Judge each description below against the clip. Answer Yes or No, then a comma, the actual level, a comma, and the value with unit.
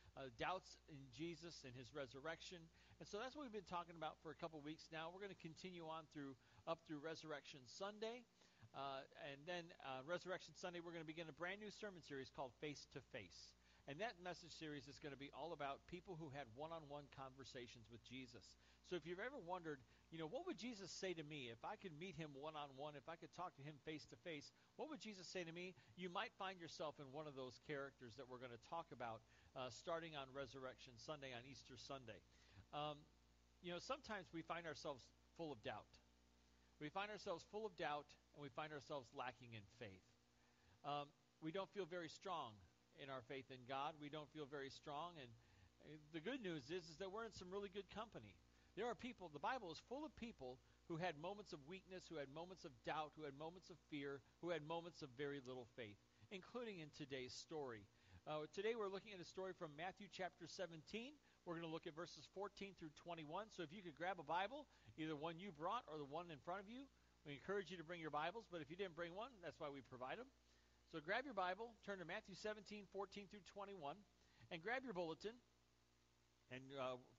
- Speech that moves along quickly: Yes, fast, 220 wpm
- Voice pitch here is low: No, medium, 160 Hz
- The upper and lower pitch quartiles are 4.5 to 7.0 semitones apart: Yes, average, 5.2 semitones